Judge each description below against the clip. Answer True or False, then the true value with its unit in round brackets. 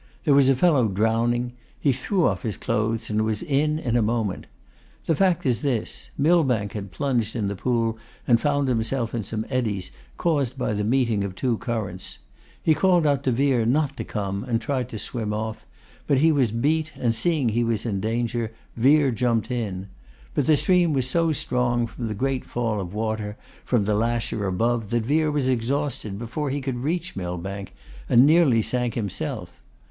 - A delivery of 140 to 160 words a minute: False (190 wpm)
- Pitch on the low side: True (120 Hz)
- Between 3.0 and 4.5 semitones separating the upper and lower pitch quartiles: True (4.2 semitones)